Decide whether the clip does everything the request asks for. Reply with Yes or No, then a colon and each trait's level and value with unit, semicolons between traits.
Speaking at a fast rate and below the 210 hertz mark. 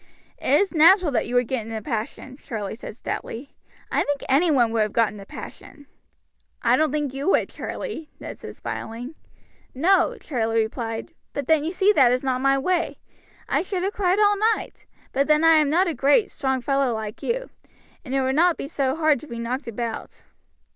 No: fast, 210 wpm; very high, 275 Hz